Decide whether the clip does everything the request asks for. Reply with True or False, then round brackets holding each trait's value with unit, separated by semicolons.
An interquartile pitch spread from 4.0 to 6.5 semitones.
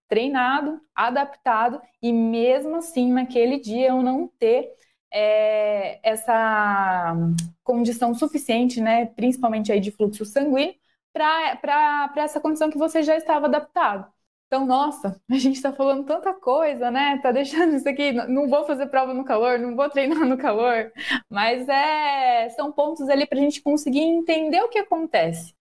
True (4.3 semitones)